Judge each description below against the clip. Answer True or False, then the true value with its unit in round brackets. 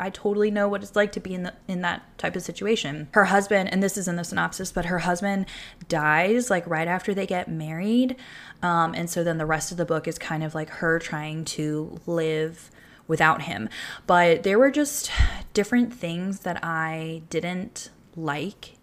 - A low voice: False (175 Hz)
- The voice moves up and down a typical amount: True (3.5 semitones)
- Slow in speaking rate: False (200 wpm)